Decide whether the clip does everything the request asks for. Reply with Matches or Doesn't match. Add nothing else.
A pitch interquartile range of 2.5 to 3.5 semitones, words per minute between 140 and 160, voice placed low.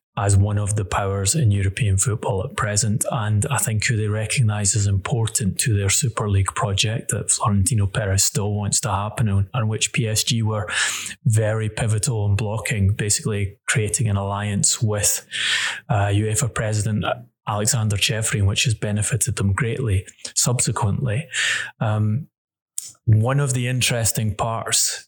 Matches